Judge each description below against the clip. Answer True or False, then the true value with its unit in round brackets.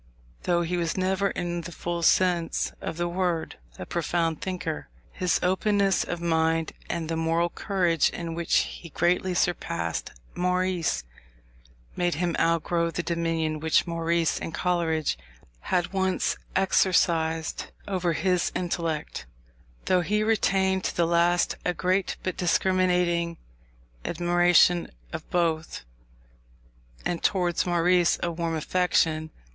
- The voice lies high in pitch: False (175 Hz)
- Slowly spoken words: True (125 wpm)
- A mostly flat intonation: True (1.6 semitones)